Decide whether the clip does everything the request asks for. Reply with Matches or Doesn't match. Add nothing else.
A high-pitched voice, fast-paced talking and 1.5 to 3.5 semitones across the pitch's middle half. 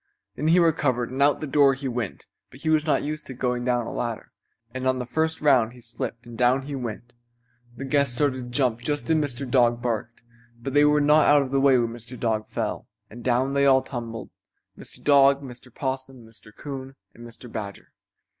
Doesn't match